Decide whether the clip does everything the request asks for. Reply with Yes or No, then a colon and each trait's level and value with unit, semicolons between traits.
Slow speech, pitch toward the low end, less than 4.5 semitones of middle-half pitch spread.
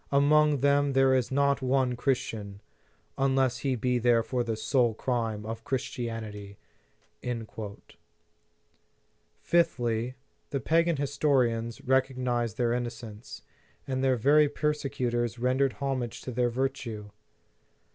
Yes: slow, 115 wpm; low, 125 Hz; average, 2.8 semitones